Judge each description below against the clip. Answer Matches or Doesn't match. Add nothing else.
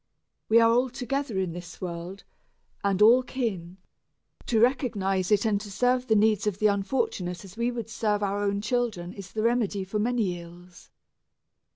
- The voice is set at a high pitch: Matches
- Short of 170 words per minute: Doesn't match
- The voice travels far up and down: Doesn't match